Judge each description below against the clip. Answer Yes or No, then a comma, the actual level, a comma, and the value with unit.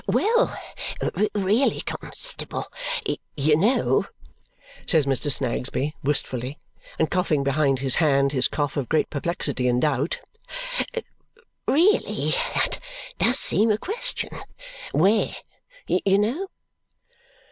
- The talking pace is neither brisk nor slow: No, slow, 105 wpm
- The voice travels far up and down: Yes, wide, 7.2 semitones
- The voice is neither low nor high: Yes, medium, 155 Hz